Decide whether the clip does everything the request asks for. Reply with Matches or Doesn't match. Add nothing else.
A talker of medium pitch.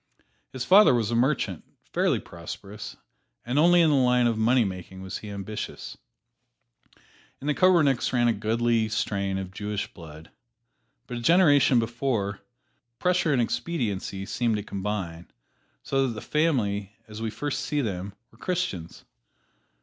Doesn't match